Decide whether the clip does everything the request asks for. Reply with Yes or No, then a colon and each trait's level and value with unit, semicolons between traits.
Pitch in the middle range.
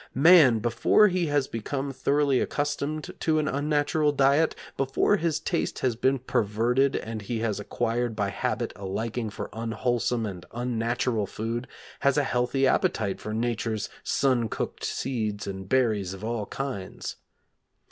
No: low, 120 Hz